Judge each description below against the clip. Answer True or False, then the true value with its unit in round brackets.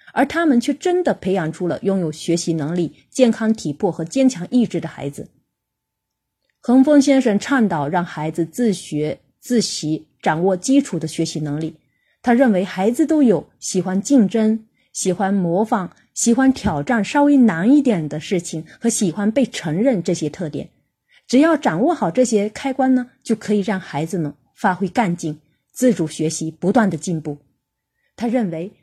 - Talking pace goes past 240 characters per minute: True (250 characters per minute)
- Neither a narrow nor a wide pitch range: False (7.2 semitones)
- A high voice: True (195 Hz)